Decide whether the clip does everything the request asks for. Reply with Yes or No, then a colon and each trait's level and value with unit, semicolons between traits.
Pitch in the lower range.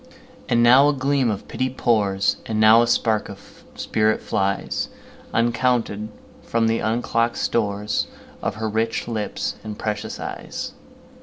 Yes: low, 115 Hz